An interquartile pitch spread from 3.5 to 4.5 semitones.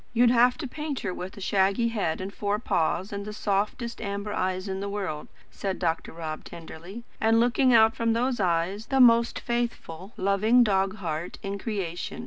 Yes: average, 3.9 semitones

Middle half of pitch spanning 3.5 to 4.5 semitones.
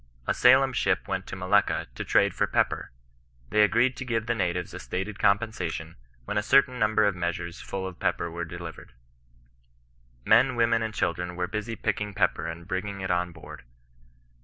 Yes: average, 4.0 semitones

